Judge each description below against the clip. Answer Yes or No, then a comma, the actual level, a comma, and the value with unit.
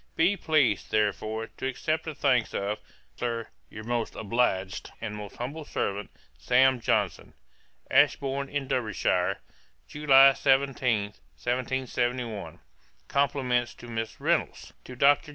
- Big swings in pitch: No, average, 3.7 semitones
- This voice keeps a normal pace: No, slow, 115 wpm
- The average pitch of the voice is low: Yes, low, 125 Hz